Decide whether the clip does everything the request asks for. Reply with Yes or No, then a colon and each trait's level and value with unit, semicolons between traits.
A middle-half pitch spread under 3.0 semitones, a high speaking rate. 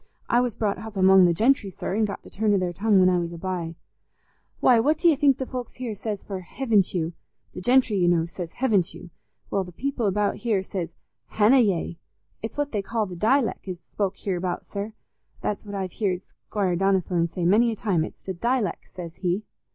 No: average, 3.8 semitones; fast, 215 wpm